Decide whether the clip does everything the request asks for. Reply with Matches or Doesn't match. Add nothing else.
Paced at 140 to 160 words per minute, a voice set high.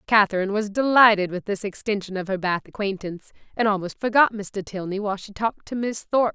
Doesn't match